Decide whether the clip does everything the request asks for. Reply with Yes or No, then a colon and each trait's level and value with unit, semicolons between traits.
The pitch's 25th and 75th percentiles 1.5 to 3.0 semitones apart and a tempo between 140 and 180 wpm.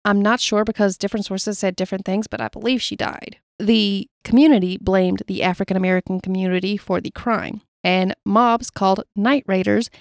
Yes: average, 2.7 semitones; average, 175 wpm